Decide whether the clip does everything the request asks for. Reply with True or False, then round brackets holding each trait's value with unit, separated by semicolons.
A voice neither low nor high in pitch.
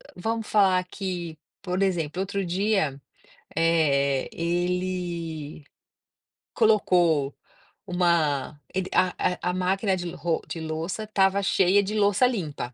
True (180 Hz)